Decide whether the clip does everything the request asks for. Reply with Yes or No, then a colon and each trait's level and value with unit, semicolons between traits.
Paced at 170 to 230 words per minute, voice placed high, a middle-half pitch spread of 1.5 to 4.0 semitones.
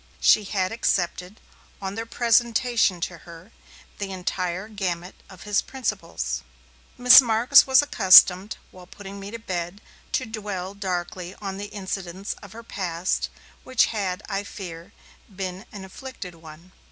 No: average, 140 wpm; high, 195 Hz; average, 3.4 semitones